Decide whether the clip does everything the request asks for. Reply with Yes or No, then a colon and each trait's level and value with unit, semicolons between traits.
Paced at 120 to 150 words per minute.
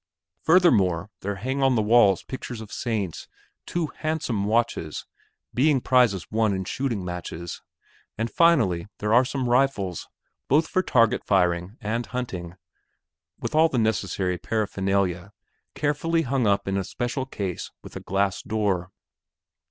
Yes: average, 140 wpm